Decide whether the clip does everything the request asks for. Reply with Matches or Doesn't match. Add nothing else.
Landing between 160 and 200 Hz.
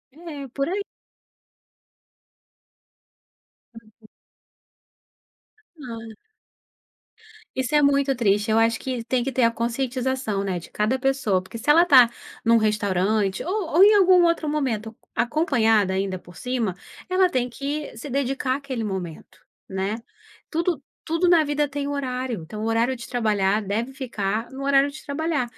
Doesn't match